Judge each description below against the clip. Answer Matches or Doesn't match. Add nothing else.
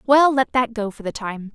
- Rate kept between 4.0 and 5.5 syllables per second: Matches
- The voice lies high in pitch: Matches